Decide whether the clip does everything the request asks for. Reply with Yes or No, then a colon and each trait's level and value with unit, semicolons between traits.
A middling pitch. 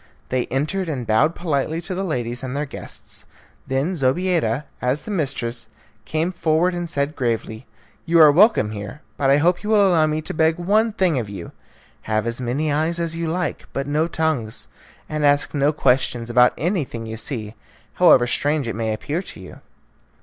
Yes: medium, 145 Hz